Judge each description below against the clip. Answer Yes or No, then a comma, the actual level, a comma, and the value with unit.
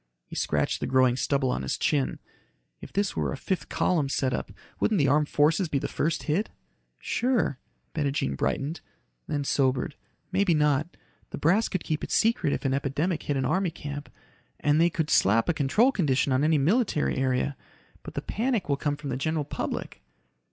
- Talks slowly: No, average, 185 wpm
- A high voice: No, medium, 150 Hz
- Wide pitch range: No, average, 4.1 semitones